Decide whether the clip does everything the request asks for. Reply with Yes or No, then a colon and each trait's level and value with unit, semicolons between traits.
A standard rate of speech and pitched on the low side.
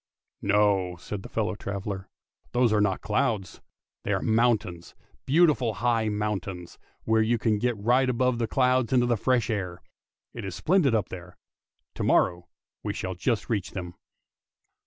Yes: average, 165 wpm; low, 110 Hz